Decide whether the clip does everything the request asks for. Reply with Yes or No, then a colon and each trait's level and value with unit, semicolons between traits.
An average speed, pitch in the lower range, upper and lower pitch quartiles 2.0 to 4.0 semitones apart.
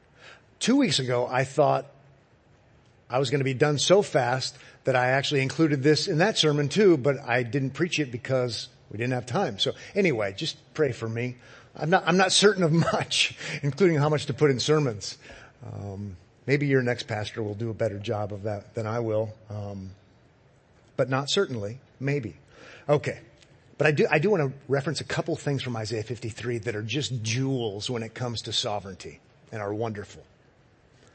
No: average, 190 wpm; low, 125 Hz; average, 4.7 semitones